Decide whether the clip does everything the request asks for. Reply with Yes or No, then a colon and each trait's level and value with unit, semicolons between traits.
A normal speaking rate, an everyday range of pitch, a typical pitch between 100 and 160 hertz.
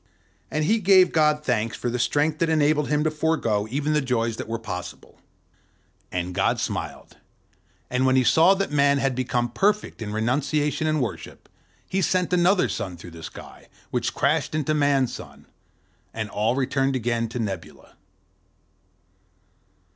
Yes: average, 160 wpm; average, 5.0 semitones; low, 135 Hz